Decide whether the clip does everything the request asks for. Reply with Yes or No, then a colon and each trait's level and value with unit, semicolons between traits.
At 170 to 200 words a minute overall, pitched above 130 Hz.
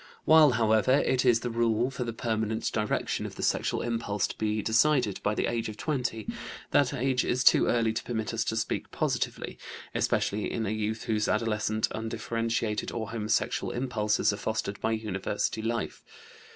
No: average, 175 wpm; low, 110 Hz